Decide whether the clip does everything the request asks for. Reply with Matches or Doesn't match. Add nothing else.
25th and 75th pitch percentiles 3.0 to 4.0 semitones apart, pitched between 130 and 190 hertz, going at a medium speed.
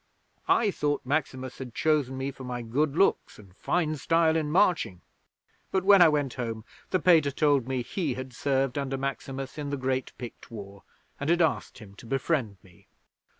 Matches